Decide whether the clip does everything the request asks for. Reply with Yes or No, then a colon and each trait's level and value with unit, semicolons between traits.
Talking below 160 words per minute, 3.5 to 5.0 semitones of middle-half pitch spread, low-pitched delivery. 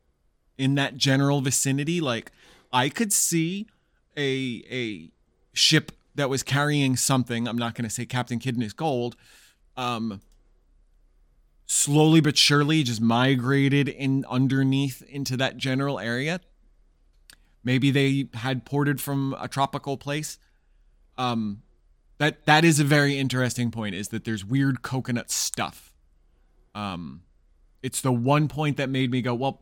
No: slow, 135 wpm; average, 3.1 semitones; low, 130 Hz